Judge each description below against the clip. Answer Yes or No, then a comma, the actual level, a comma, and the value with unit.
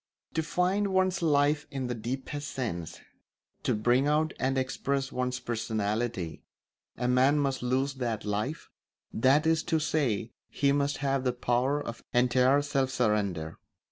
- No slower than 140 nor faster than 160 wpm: Yes, average, 145 wpm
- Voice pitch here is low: Yes, low, 130 Hz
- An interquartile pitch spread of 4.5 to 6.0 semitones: No, average, 3.1 semitones